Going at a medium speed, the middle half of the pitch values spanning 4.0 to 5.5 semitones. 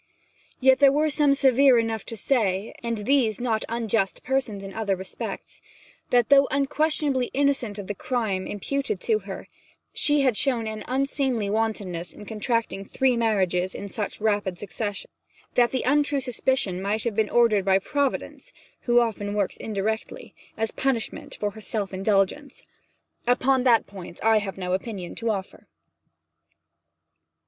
Yes: average, 155 wpm; average, 4.5 semitones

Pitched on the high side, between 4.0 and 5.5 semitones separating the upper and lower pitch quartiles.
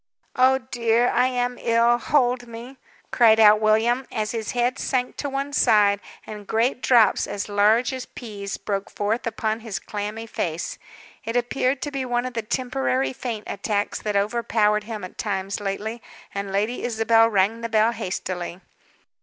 No: high, 225 Hz; average, 2.7 semitones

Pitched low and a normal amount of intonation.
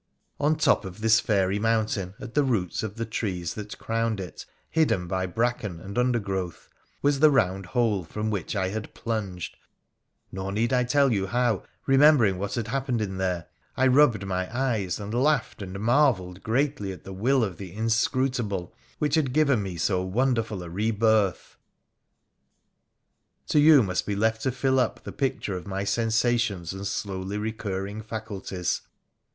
Yes: low, 110 Hz; average, 4.3 semitones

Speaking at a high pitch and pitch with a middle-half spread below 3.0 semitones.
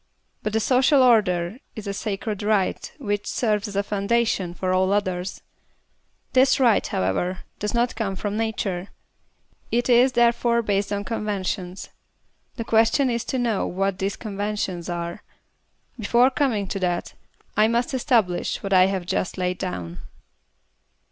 No: high, 205 Hz; average, 3.9 semitones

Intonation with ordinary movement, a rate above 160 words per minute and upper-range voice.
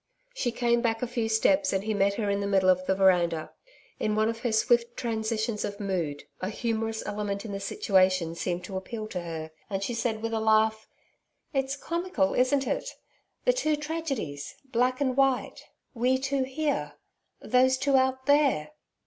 Yes: average, 4.9 semitones; average, 180 wpm; high, 225 Hz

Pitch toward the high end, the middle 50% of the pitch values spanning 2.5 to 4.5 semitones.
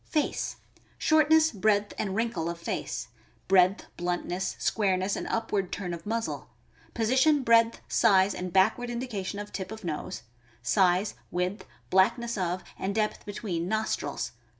Yes: high, 200 Hz; average, 3.7 semitones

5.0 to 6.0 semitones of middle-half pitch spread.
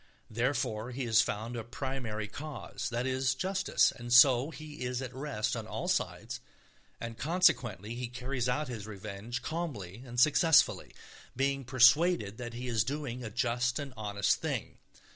No: average, 3.0 semitones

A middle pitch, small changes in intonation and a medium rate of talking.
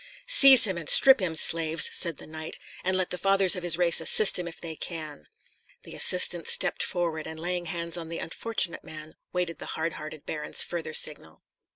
Yes: medium, 170 Hz; narrow, 2.3 semitones; average, 195 wpm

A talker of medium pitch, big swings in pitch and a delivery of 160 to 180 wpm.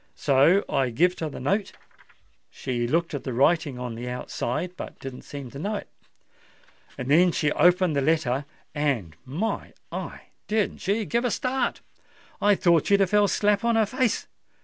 Yes: medium, 160 Hz; wide, 7.1 semitones; average, 170 wpm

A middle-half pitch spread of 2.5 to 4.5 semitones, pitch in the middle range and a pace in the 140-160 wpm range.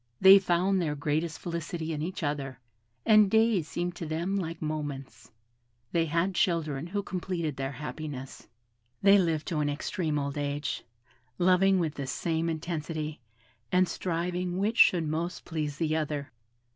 Yes: average, 3.3 semitones; medium, 165 Hz; average, 150 wpm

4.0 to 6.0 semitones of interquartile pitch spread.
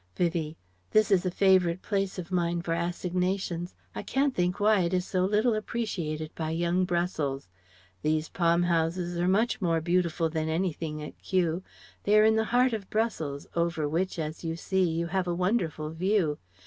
No: average, 2.8 semitones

